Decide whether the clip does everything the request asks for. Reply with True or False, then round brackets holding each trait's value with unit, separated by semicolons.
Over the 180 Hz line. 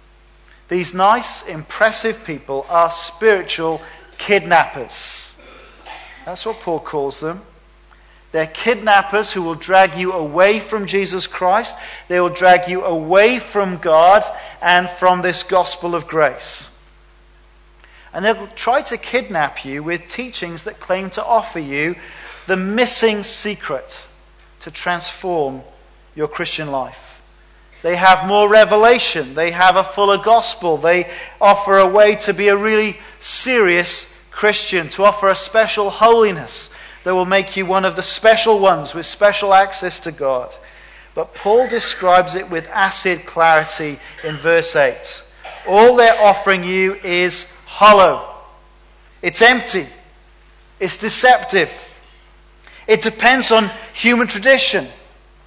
True (190 Hz)